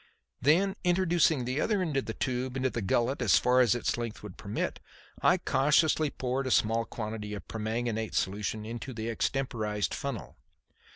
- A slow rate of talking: No, average, 175 wpm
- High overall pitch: No, low, 120 Hz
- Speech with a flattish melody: No, average, 3.7 semitones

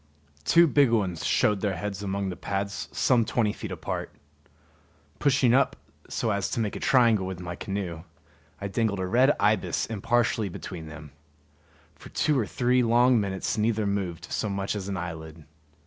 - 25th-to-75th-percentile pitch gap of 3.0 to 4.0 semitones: Yes, average, 3.7 semitones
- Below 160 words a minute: No, average, 170 wpm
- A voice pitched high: No, low, 100 Hz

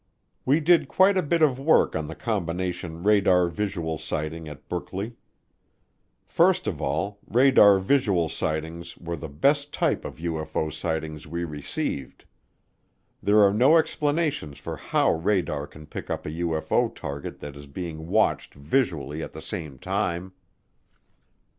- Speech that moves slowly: No, average, 145 wpm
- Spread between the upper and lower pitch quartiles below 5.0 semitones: No, wide, 5.4 semitones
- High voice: No, very low, 85 Hz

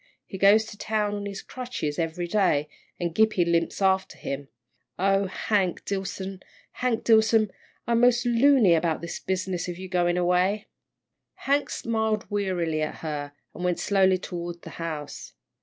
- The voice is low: No, high, 190 Hz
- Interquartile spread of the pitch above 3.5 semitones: Yes, average, 3.9 semitones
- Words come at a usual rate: Yes, average, 155 wpm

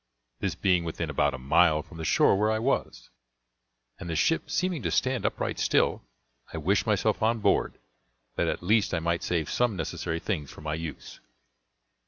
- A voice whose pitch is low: Yes, very low, 90 Hz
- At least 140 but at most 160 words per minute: No, average, 185 wpm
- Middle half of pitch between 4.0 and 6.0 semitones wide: Yes, average, 5.3 semitones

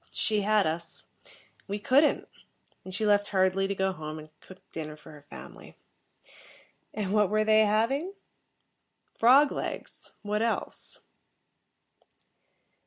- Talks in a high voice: Yes, high, 205 Hz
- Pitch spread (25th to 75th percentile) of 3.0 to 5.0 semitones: No, narrow, 2.6 semitones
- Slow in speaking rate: Yes, slow, 125 wpm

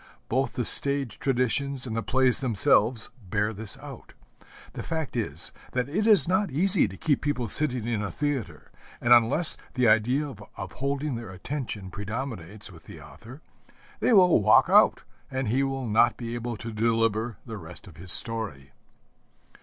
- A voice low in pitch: Yes, low, 120 Hz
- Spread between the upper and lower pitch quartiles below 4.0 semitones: No, average, 4.4 semitones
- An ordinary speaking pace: Yes, average, 170 wpm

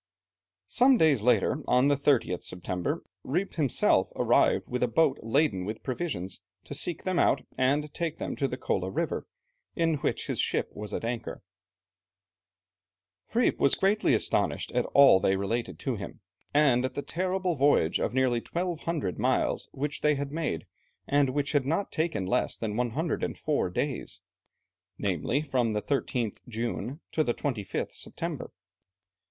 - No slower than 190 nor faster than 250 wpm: No, average, 155 wpm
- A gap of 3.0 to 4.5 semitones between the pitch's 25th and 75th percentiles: No, average, 5.3 semitones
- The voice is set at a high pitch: No, low, 135 Hz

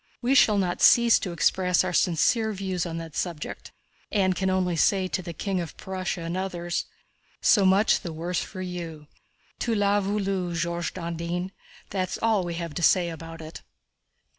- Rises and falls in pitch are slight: Yes, narrow, 2.2 semitones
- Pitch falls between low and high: Yes, medium, 180 Hz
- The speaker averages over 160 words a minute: Yes, average, 175 wpm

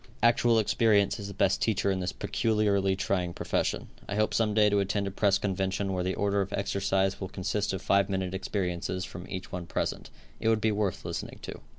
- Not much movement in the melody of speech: Yes, narrow, 1.8 semitones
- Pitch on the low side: Yes, low, 100 Hz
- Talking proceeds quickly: Yes, fast, 210 wpm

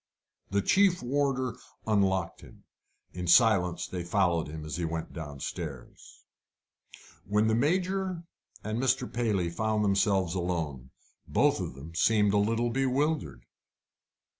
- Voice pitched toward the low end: Yes, low, 100 Hz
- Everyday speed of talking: No, slow, 125 wpm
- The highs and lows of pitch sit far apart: Yes, wide, 6.3 semitones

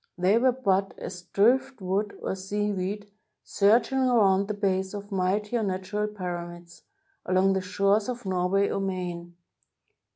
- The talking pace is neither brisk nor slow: No, slow, 130 wpm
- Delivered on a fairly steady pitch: Yes, narrow, 2.1 semitones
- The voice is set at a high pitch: Yes, high, 195 Hz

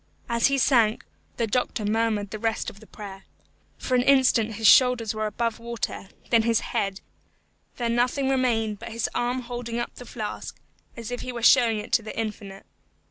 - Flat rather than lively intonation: Yes, narrow, 2.3 semitones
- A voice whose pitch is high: Yes, high, 230 Hz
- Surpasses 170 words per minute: Yes, average, 190 wpm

